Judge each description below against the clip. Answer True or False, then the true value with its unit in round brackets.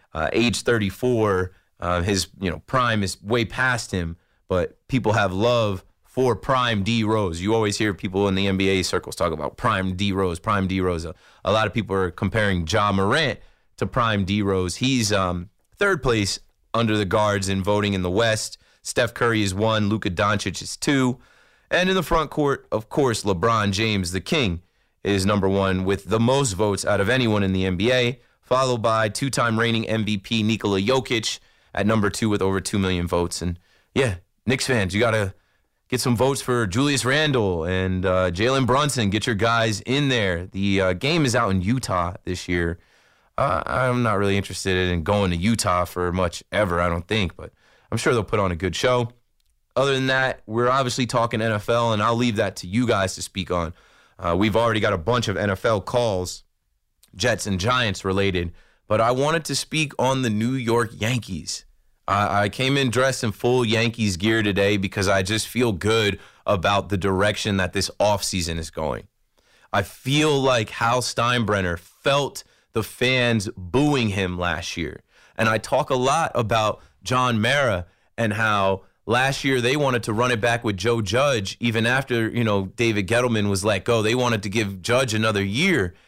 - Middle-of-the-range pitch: False (105 Hz)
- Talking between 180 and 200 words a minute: True (190 wpm)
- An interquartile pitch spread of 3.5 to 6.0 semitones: True (3.9 semitones)